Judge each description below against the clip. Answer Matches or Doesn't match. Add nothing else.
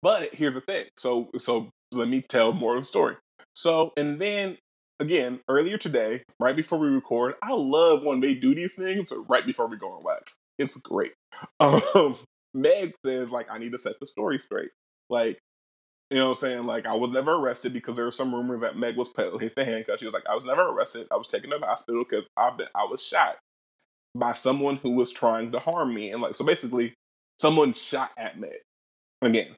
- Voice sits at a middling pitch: Doesn't match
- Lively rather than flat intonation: Matches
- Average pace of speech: Doesn't match